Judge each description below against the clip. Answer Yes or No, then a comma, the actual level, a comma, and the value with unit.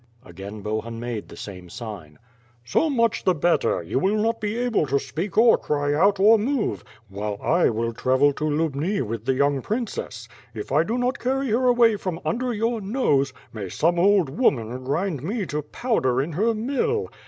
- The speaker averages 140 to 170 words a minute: No, average, 190 wpm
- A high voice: No, medium, 160 Hz